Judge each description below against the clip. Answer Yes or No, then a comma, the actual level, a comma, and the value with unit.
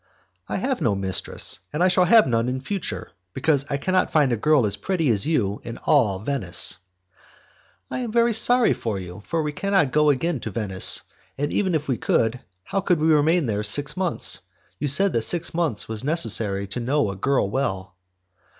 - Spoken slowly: No, average, 200 wpm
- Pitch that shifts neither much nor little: No, wide, 7.4 semitones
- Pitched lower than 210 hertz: Yes, medium, 140 Hz